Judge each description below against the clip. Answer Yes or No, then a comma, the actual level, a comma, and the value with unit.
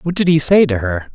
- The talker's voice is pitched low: No, medium, 145 Hz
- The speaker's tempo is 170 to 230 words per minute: No, fast, 315 wpm